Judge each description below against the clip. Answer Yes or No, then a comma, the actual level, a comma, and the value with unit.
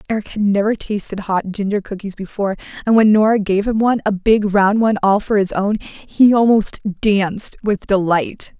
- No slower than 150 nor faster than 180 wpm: No, average, 190 wpm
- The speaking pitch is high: Yes, high, 205 Hz